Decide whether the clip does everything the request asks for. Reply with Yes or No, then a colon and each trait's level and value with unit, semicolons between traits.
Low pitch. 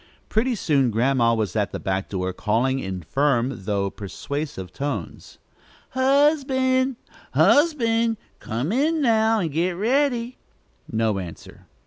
No: medium, 145 Hz